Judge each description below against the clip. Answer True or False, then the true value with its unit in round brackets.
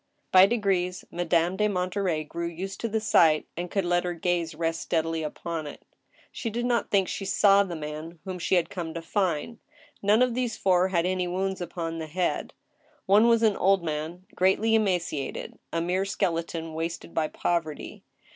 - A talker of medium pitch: True (180 Hz)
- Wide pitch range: False (3.0 semitones)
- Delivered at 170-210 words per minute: True (185 wpm)